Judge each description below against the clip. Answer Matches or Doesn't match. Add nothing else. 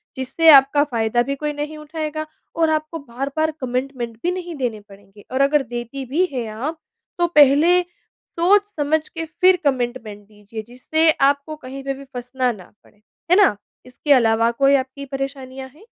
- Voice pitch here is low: Doesn't match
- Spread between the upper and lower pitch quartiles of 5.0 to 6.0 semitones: Doesn't match